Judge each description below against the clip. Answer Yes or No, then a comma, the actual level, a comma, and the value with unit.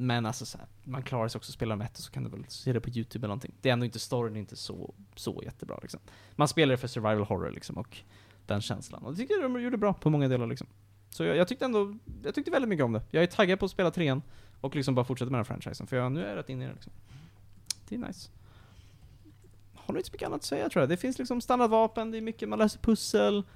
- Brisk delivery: Yes, fast, 290 wpm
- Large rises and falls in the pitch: Yes, wide, 8.1 semitones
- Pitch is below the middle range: Yes, low, 120 Hz